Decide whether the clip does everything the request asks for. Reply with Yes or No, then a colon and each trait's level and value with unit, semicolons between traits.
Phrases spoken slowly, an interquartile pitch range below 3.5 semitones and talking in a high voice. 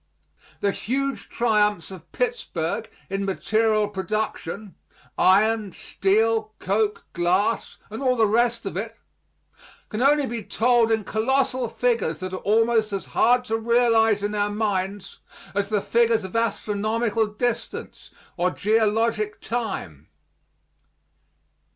Yes: slow, 120 wpm; narrow, 2.4 semitones; high, 220 Hz